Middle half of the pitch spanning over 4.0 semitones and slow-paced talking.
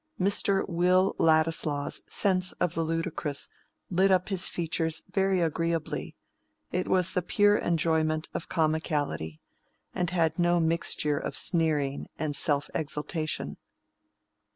No: narrow, 2.6 semitones; slow, 120 wpm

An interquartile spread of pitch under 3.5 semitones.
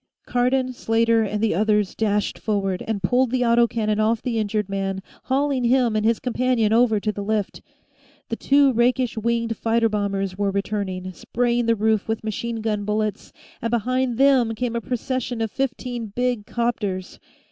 Yes: average, 2.7 semitones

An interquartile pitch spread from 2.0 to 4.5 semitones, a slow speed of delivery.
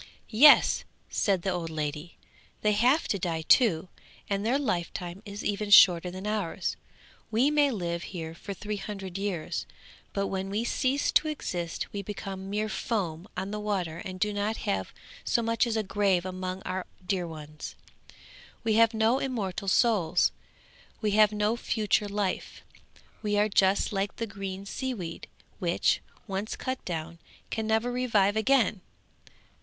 No: average, 3.1 semitones; average, 160 wpm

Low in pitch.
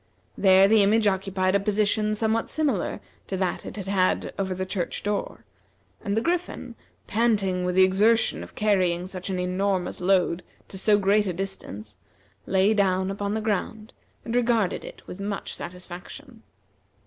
No: high, 195 Hz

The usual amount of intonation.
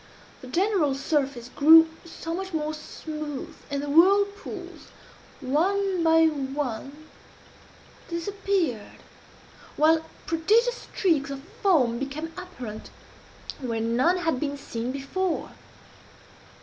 Yes: average, 4.5 semitones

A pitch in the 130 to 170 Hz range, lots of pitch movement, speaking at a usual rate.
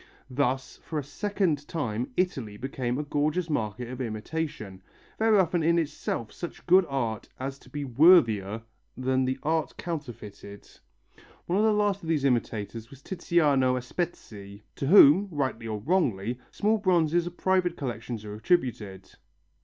Yes: medium, 140 Hz; wide, 6.9 semitones; average, 150 wpm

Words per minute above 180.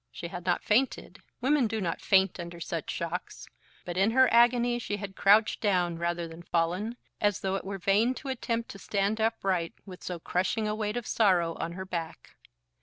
Yes: average, 195 wpm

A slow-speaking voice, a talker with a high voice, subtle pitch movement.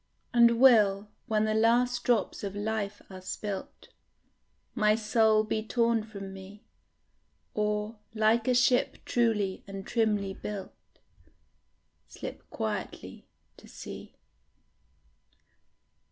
Yes: slow, 105 wpm; high, 215 Hz; narrow, 2.2 semitones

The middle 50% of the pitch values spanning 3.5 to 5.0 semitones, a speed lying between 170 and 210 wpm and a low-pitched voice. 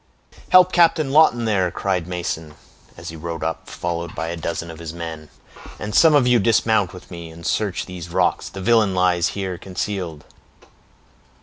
Yes: average, 4.4 semitones; average, 175 wpm; very low, 90 Hz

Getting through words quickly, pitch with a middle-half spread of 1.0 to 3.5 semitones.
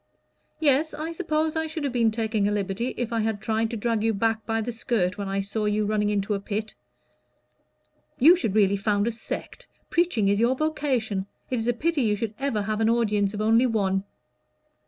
Yes: fast, 210 wpm; average, 3.2 semitones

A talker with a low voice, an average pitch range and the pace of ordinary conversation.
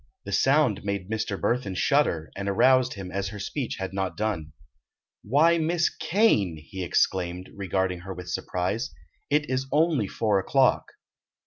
No: low, 100 Hz; wide, 5.9 semitones; average, 150 wpm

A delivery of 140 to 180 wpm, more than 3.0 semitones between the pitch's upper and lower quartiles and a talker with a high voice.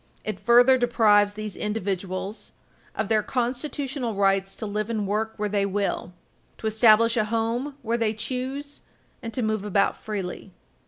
No: average, 155 wpm; narrow, 2.5 semitones; high, 220 Hz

